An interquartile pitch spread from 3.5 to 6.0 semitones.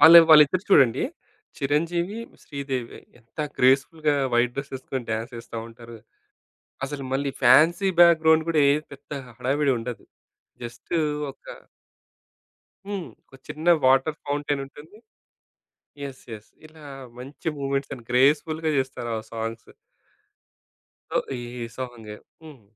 Yes: average, 4.1 semitones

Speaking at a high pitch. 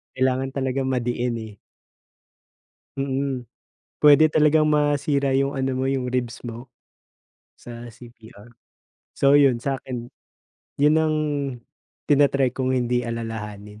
No: low, 130 Hz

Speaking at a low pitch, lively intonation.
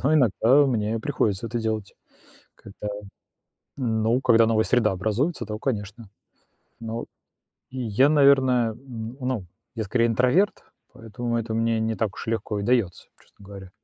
No: low, 115 Hz; average, 2.7 semitones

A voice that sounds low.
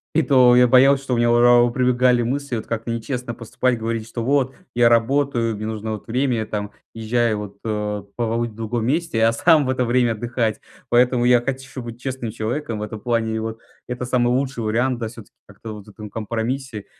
Yes: low, 120 Hz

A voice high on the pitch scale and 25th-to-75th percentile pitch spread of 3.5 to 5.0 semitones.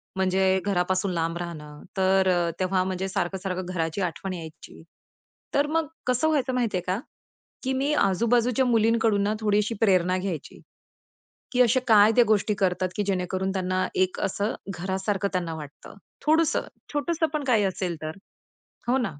Yes: high, 195 Hz; average, 3.9 semitones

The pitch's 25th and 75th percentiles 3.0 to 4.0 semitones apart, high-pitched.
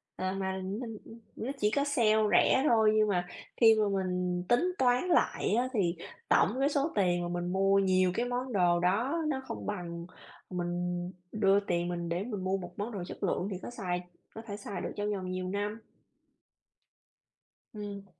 Yes: average, 3.7 semitones; high, 200 Hz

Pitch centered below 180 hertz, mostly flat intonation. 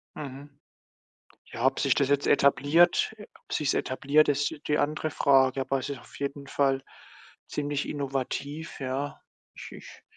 Yes: medium, 140 Hz; narrow, 1.4 semitones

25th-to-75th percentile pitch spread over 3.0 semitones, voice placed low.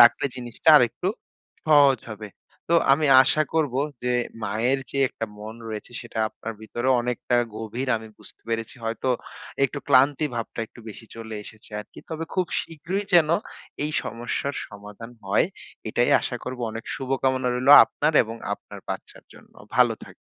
Yes: average, 3.7 semitones; low, 125 Hz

